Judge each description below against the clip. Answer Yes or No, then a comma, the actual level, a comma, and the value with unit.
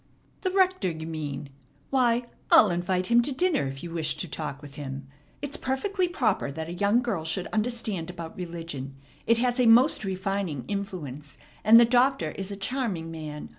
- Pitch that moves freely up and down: Yes, wide, 7.0 semitones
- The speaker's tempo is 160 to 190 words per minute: Yes, average, 180 wpm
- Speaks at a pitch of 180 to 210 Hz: Yes, high, 190 Hz